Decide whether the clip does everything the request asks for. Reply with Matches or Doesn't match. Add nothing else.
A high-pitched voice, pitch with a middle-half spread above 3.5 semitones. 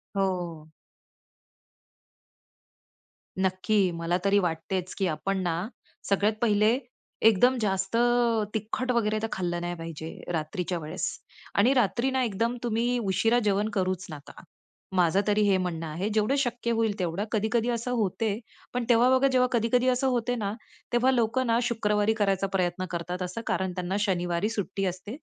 Matches